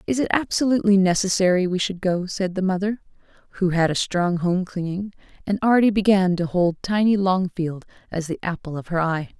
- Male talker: No, female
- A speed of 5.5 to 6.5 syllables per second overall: Yes, 5.6 syllables/s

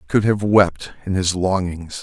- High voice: No, very low, 95 Hz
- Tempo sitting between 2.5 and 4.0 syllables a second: No, 4.9 syllables/s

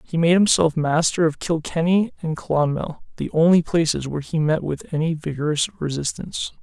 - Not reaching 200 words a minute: Yes, average, 165 wpm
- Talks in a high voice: No, medium, 160 Hz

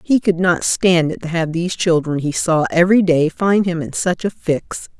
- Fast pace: Yes, fast, 230 wpm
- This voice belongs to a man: No, female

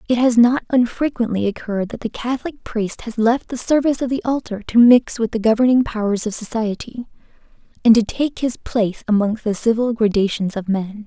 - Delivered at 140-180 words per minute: No, average, 190 wpm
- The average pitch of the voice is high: Yes, high, 230 Hz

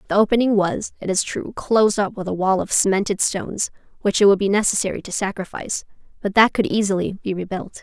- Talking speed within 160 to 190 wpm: No, fast, 205 wpm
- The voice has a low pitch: No, high, 200 Hz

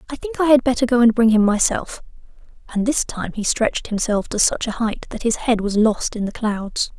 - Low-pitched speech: No, high, 225 Hz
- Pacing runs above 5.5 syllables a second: No, 5.4 syllables/s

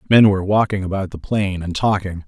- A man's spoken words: Yes, male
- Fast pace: Yes, fast, 210 wpm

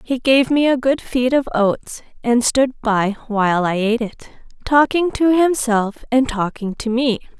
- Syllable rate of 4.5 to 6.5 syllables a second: No, 4.2 syllables/s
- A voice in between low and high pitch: No, high, 245 Hz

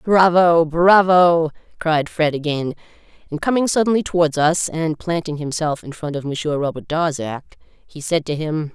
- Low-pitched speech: No, medium, 160 Hz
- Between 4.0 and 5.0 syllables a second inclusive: Yes, 4.5 syllables/s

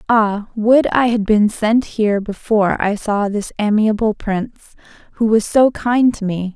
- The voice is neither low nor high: No, high, 215 Hz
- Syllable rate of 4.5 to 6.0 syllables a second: No, 4.3 syllables/s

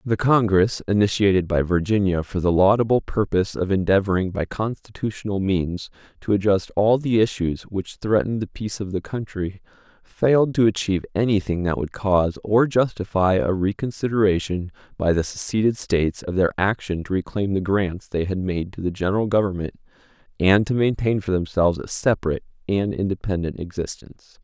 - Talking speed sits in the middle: Yes, average, 160 wpm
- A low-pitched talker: Yes, low, 100 Hz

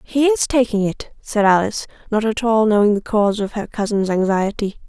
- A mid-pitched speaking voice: No, high, 215 Hz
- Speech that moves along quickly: No, average, 195 wpm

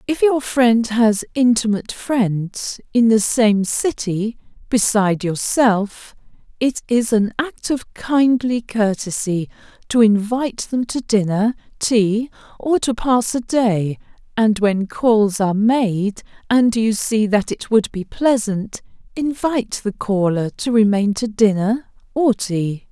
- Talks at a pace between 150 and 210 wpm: No, slow, 135 wpm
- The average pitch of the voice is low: No, high, 225 Hz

